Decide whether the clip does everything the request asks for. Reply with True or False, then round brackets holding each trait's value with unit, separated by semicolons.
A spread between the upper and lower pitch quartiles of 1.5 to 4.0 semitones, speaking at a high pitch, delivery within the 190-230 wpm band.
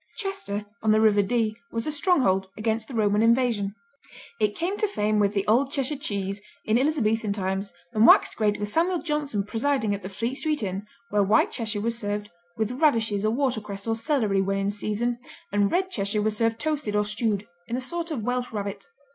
True (3.7 semitones; 220 Hz; 200 wpm)